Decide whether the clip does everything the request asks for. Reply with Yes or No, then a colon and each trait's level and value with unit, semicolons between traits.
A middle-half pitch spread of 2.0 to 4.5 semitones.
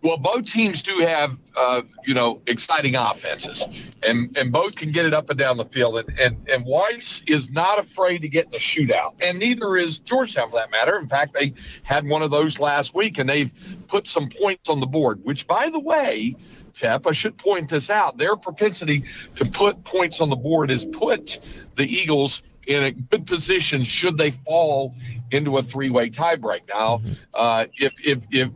No: wide, 5.6 semitones